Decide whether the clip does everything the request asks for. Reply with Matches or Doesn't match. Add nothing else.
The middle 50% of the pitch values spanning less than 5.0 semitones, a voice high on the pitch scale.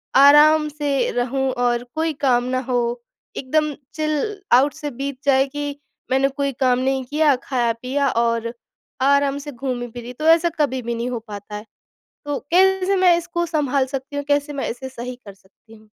Matches